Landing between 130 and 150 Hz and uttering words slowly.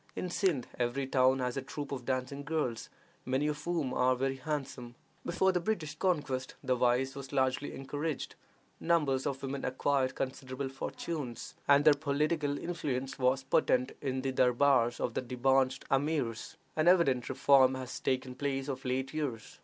No: low, 135 Hz; average, 165 wpm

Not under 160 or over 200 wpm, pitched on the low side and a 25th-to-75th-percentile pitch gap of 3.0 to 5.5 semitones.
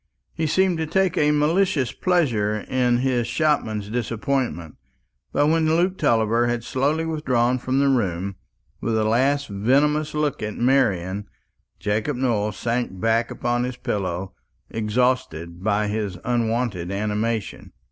No: slow, 135 wpm; low, 120 Hz; average, 5.1 semitones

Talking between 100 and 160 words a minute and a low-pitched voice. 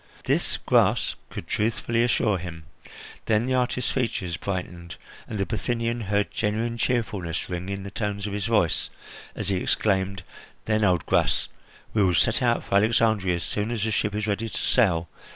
No: average, 175 wpm; low, 105 Hz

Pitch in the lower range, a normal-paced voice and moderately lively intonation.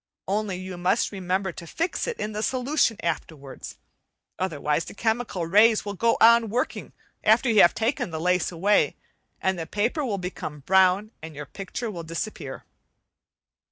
No: high, 195 Hz; average, 165 wpm; average, 4.6 semitones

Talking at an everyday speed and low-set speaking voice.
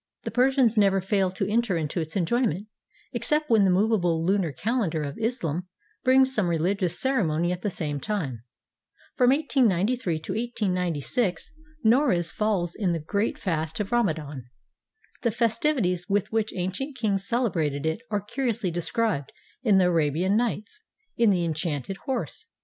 No: average, 150 wpm; high, 195 Hz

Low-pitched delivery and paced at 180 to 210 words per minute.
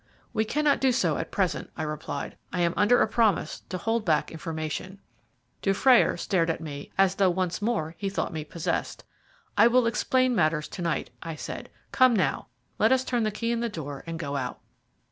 No: high, 190 Hz; average, 200 wpm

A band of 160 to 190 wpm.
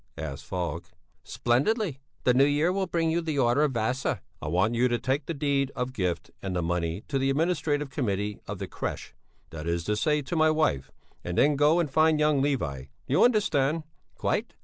No: fast, 205 wpm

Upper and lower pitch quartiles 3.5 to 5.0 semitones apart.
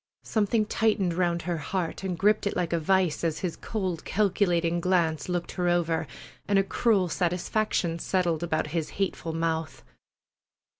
No: average, 2.7 semitones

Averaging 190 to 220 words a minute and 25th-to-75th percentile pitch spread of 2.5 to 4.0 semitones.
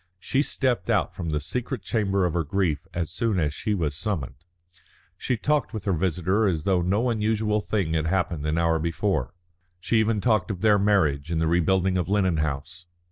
No: average, 195 wpm; average, 4.6 semitones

